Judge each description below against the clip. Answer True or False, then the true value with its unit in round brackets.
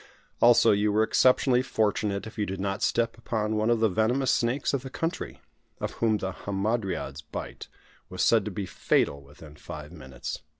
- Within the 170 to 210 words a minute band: True (180 wpm)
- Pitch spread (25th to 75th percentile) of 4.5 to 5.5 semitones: False (3.4 semitones)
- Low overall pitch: True (105 Hz)